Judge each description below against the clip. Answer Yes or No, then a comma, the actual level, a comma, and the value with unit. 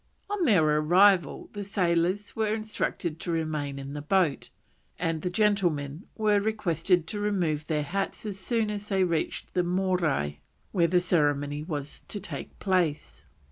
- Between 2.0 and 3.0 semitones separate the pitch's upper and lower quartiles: No, average, 4.8 semitones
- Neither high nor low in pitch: Yes, medium, 180 Hz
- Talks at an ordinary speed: Yes, average, 155 wpm